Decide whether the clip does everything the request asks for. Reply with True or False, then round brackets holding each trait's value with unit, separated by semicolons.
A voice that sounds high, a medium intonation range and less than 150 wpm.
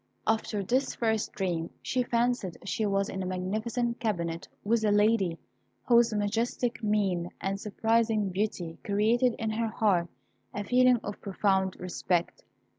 True (210 Hz; 3.2 semitones; 140 wpm)